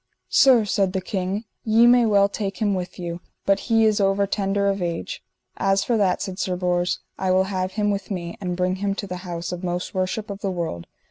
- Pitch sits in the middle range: No, high, 195 Hz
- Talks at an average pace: No, fast, 225 wpm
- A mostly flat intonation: Yes, narrow, 2.0 semitones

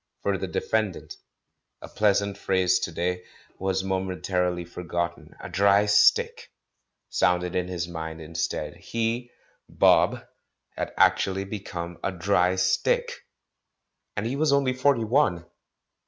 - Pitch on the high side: No, very low, 95 Hz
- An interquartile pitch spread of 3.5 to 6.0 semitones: No, average, 2.7 semitones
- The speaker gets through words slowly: Yes, slow, 125 wpm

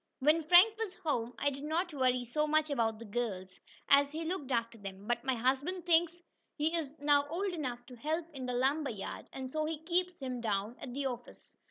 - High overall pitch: Yes, very high, 280 Hz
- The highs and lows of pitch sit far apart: No, average, 4.7 semitones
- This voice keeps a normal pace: No, fast, 215 wpm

